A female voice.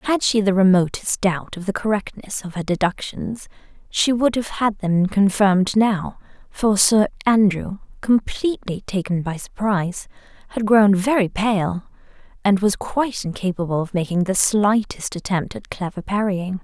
Yes: female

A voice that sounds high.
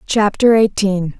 Yes: high, 205 Hz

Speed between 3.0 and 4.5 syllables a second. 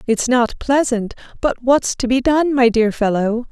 Yes: 4.3 syllables/s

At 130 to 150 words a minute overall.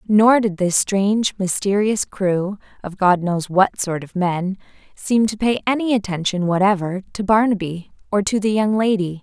No: average, 170 wpm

